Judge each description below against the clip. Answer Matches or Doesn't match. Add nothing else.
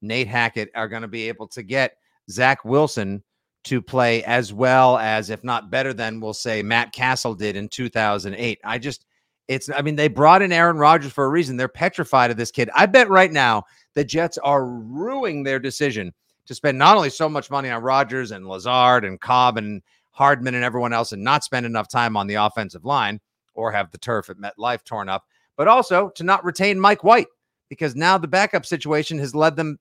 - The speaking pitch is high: Doesn't match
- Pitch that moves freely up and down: Doesn't match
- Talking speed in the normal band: Doesn't match